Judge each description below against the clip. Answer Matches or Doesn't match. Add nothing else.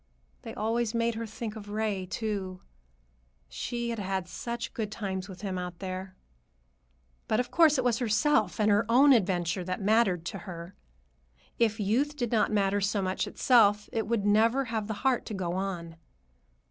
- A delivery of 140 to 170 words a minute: Doesn't match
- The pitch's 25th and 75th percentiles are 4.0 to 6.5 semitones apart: Doesn't match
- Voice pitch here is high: Matches